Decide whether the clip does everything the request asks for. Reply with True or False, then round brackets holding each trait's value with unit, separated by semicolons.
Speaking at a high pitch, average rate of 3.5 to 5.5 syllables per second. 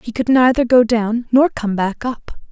True (235 Hz; 4.5 syllables/s)